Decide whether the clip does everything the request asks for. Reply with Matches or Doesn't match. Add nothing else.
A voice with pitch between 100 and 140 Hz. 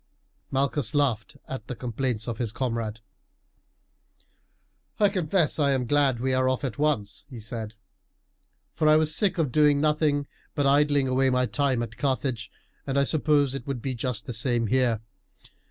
Matches